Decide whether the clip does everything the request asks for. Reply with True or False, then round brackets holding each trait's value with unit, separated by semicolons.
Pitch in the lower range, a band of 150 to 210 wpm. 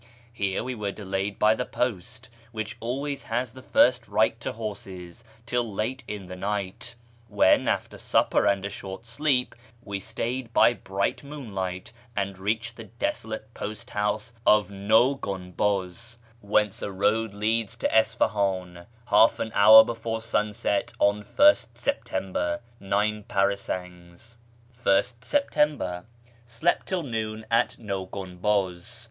False (105 Hz; 135 wpm)